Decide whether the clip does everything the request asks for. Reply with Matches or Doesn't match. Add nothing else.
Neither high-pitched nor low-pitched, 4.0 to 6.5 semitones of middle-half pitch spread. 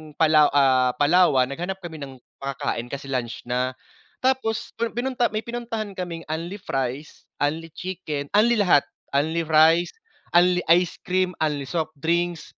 Matches